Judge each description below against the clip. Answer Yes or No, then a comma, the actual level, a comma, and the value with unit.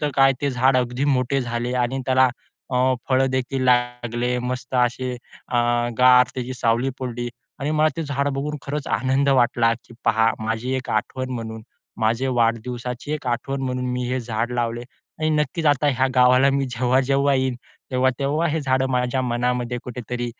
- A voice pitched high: No, low, 125 Hz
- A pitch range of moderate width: No, narrow, 1.7 semitones